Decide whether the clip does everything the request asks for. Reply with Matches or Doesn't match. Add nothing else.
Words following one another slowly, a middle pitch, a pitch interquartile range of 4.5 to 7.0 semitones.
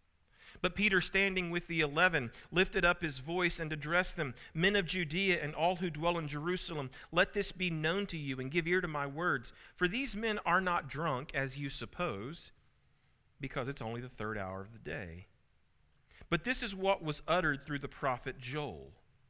Doesn't match